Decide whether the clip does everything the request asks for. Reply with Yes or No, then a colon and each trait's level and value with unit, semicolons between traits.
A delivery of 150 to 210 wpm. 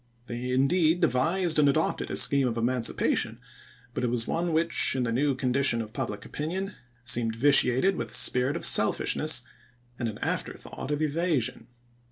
Yes: average, 165 wpm